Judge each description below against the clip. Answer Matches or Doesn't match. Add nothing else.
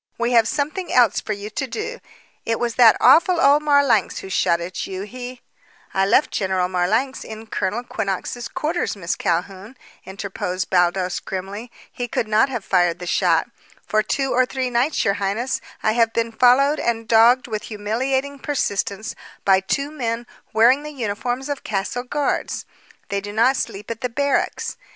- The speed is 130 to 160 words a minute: Doesn't match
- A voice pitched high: Matches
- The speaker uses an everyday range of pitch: Matches